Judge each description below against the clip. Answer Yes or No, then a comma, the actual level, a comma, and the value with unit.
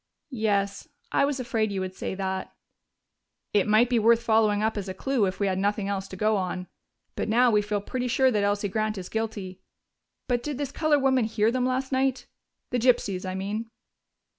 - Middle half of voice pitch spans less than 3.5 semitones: No, average, 3.9 semitones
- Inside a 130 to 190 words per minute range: No, fast, 205 wpm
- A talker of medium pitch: No, high, 215 Hz